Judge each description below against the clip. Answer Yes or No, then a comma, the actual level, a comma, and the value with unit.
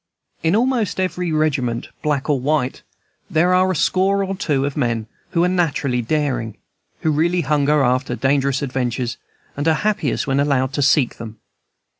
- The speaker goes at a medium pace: Yes, average, 165 wpm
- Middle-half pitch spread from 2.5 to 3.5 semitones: No, average, 4.6 semitones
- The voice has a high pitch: No, medium, 145 Hz